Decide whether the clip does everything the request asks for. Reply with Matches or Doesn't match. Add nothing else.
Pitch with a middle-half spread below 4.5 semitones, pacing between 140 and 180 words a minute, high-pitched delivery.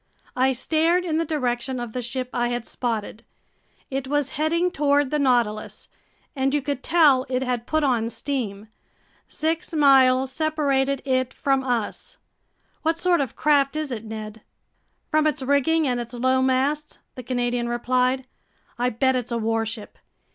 Matches